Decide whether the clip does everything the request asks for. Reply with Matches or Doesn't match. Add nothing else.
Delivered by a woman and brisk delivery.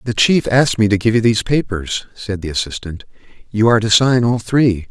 Doesn't match